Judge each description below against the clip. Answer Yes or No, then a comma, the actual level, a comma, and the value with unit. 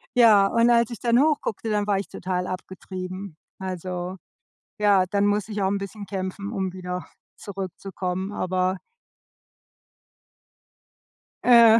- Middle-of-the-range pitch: No, high, 195 Hz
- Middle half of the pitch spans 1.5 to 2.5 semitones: Yes, narrow, 2.2 semitones